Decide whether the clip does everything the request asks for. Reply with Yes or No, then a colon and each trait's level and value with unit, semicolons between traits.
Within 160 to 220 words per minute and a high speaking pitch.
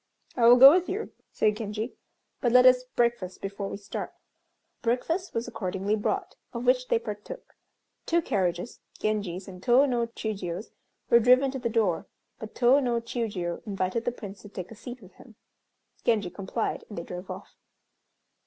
Yes: average, 170 wpm; high, 225 Hz